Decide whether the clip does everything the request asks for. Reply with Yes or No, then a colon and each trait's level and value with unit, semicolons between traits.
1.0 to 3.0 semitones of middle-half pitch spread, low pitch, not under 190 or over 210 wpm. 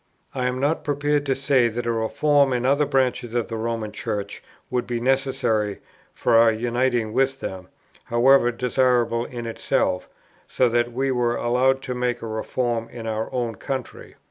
No: narrow, 2.4 semitones; low, 120 Hz; average, 170 wpm